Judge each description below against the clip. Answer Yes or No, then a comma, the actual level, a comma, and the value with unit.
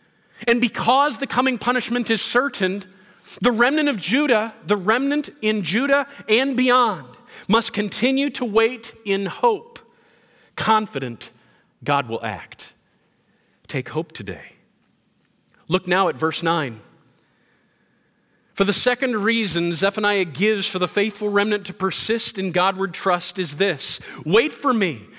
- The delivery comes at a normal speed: No, slow, 130 wpm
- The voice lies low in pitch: No, high, 205 Hz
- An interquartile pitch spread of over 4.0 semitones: Yes, average, 5.0 semitones